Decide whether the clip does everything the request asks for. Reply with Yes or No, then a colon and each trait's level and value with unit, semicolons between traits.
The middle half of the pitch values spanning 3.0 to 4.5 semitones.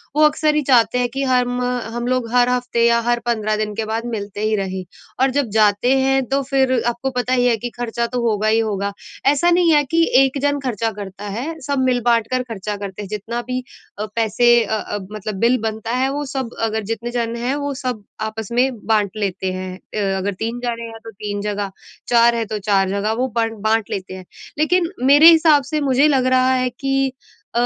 Yes: average, 3.5 semitones